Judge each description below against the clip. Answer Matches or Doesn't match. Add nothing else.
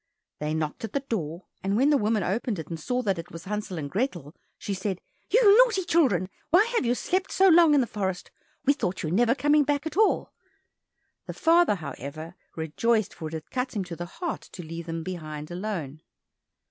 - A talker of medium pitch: Doesn't match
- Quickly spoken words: Matches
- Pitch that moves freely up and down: Matches